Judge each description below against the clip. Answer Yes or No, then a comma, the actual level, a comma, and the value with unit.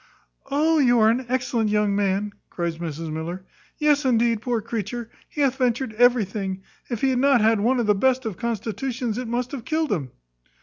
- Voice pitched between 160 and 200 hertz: No, high, 235 Hz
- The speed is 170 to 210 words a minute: Yes, average, 190 wpm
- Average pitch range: Yes, average, 3.7 semitones